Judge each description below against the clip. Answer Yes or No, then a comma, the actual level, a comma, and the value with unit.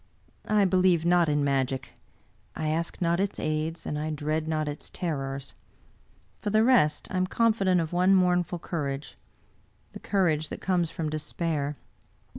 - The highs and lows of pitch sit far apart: No, average, 3.4 semitones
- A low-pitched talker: No, medium, 165 Hz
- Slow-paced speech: No, average, 160 wpm